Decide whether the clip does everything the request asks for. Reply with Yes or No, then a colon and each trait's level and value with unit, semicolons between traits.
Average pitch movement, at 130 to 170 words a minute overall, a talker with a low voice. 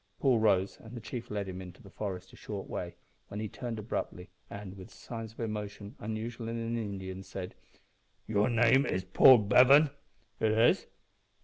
No: average, 3.1 semitones; average, 180 wpm; low, 105 Hz